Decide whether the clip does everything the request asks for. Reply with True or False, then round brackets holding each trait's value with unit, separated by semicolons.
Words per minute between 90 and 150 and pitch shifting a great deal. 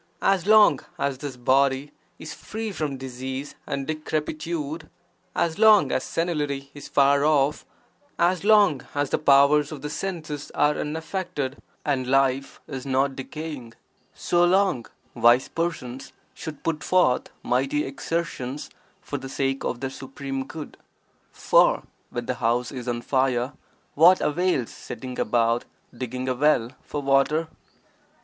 False (140 wpm; 3.2 semitones)